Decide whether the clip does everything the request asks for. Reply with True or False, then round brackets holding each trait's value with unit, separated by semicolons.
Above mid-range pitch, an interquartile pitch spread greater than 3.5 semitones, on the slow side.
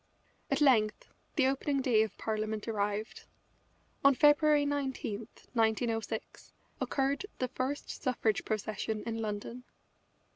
True (230 Hz; 4.1 semitones; 110 wpm)